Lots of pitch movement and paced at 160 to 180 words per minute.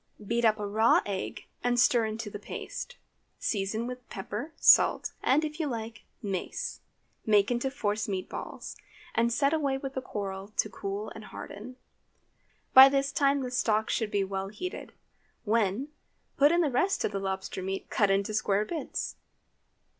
No: average, 4.8 semitones; average, 170 wpm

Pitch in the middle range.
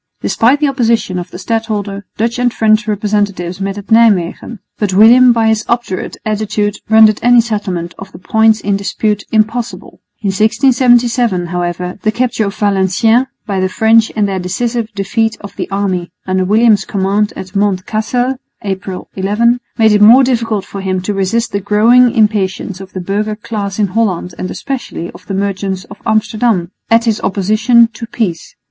No: high, 210 Hz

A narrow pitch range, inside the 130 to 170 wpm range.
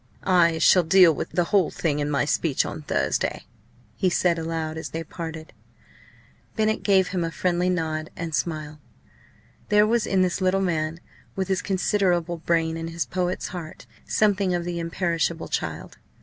Yes: narrow, 2.3 semitones; average, 165 wpm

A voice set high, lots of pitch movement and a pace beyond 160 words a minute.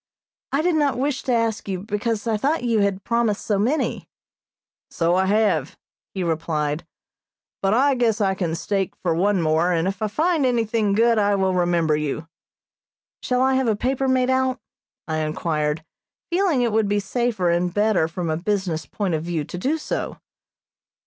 Yes: high, 205 Hz; wide, 5.9 semitones; average, 180 wpm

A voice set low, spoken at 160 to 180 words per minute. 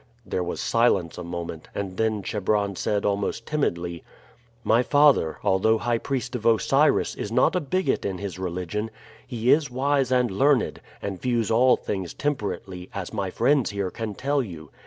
Yes: low, 110 Hz; average, 170 wpm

